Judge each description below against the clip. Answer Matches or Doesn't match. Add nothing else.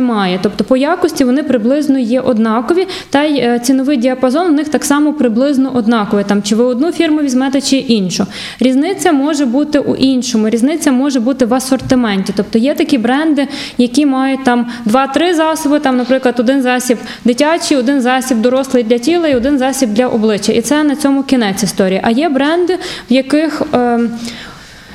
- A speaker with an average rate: Doesn't match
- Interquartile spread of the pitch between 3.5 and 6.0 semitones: Doesn't match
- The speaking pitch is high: Matches